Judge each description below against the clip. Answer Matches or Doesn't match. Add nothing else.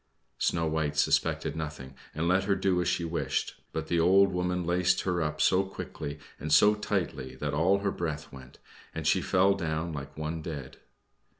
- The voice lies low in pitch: Matches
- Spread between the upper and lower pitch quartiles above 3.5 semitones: Doesn't match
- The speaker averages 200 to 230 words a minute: Doesn't match